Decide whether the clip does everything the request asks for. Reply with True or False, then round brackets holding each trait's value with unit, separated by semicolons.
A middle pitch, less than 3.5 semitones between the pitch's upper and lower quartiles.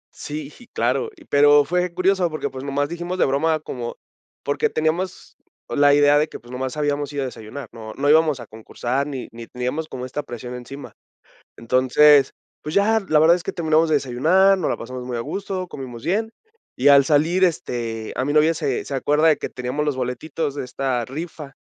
False (145 Hz; 3.9 semitones)